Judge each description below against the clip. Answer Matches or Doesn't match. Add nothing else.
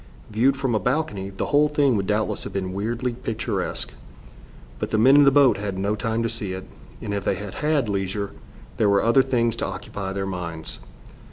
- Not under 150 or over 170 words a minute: Doesn't match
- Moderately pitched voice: Doesn't match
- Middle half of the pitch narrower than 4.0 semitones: Doesn't match